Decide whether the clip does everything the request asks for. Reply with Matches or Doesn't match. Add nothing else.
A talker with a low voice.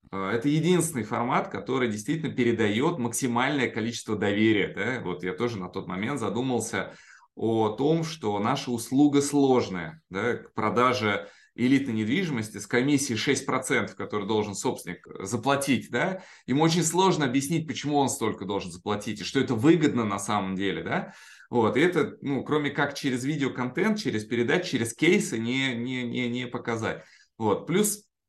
Matches